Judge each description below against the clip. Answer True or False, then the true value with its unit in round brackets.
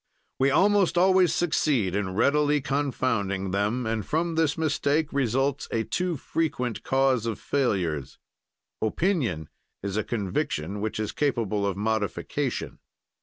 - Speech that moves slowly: True (125 wpm)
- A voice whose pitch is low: True (125 Hz)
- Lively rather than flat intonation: True (6.4 semitones)